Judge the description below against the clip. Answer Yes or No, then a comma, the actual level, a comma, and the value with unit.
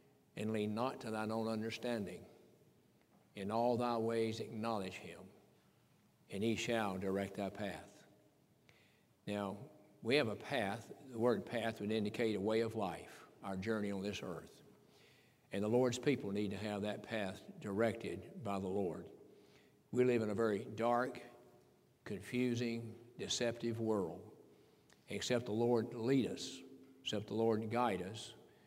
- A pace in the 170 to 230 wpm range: No, average, 145 wpm